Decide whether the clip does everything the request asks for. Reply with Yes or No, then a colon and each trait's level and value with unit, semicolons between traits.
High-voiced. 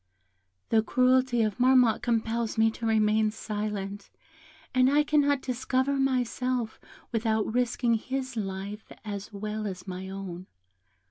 Yes: high, 225 Hz